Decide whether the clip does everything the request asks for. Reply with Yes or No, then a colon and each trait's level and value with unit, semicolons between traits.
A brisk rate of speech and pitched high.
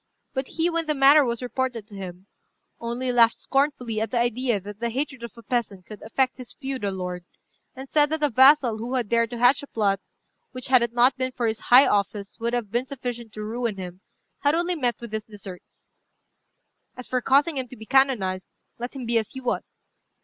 Yes: fast, 215 wpm; high, 240 Hz